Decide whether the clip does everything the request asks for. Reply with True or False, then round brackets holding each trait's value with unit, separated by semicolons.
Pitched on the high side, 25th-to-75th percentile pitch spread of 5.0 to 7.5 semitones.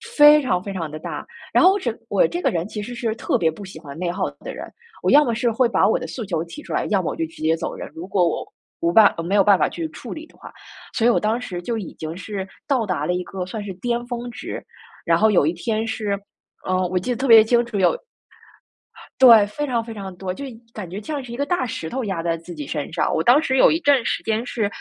True (210 Hz; 5.3 semitones)